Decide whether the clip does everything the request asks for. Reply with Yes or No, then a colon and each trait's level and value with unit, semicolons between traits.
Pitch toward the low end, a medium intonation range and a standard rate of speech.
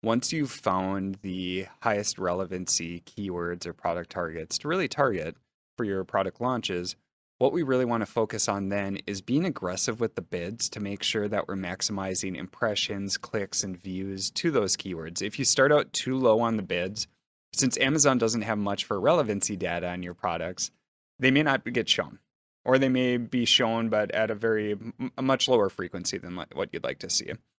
Yes: low, 100 Hz; average, 4.0 semitones; average, 190 wpm